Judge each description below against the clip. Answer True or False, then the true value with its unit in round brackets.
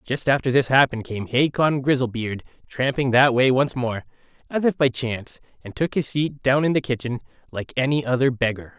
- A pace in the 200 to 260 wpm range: False (190 wpm)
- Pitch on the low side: True (130 Hz)